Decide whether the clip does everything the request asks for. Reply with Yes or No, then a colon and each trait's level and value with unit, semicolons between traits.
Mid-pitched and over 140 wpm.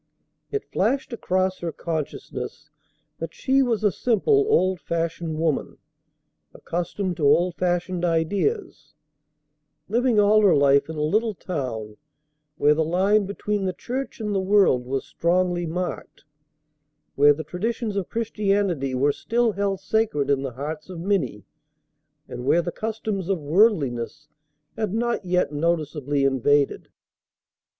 No: medium, 180 Hz; slow, 135 wpm